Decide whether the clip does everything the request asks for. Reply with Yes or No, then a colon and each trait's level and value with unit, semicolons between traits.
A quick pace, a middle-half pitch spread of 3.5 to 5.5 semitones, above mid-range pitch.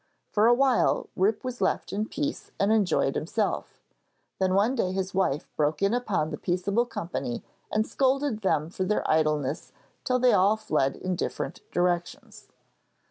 No: average, 160 wpm; average, 4.9 semitones; high, 195 Hz